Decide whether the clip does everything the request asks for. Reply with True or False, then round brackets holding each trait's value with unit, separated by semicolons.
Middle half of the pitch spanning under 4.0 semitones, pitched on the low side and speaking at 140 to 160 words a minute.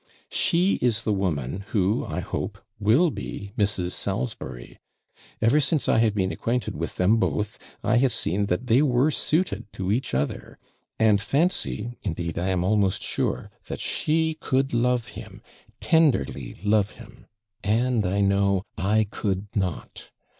False (4.5 semitones; 105 Hz; 150 wpm)